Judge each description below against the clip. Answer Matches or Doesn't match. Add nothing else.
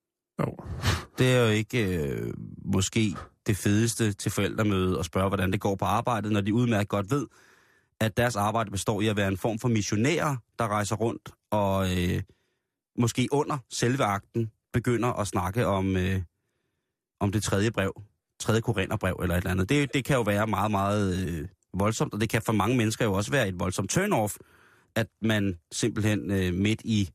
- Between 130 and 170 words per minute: Doesn't match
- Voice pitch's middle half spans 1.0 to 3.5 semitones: Matches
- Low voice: Matches